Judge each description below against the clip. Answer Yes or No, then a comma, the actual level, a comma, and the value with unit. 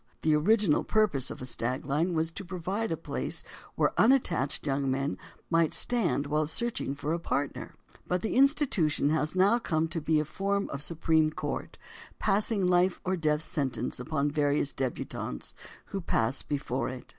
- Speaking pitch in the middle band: Yes, medium, 160 Hz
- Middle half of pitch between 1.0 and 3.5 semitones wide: No, average, 4.8 semitones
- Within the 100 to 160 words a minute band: No, average, 170 wpm